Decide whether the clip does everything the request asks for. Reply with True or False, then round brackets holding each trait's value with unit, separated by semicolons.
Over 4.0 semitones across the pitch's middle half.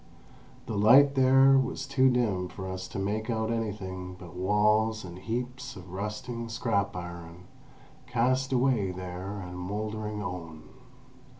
True (4.7 semitones)